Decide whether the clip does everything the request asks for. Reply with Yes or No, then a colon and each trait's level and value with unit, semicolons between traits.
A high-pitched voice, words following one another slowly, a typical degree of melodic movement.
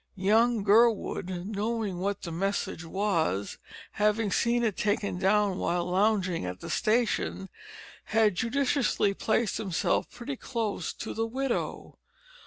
Yes: high, 210 Hz; slow, 125 wpm; average, 3.3 semitones